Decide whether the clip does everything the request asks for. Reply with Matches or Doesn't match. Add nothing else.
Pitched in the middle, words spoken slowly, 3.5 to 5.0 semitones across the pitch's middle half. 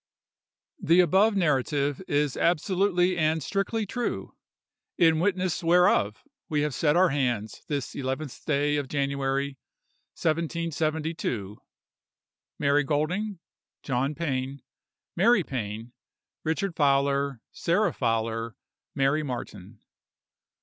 Matches